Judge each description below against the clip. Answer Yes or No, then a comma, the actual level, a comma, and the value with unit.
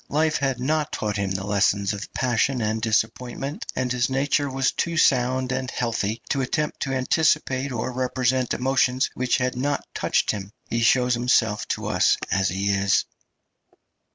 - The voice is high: No, low, 125 Hz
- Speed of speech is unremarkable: Yes, average, 165 wpm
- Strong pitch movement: No, average, 3.4 semitones